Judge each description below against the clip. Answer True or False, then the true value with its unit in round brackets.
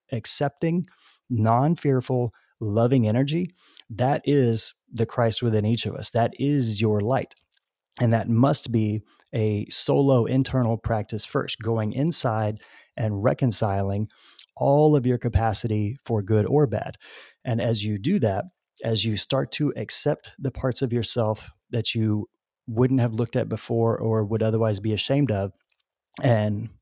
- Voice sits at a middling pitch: False (115 Hz)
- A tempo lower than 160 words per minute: True (150 wpm)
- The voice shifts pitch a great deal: False (3.4 semitones)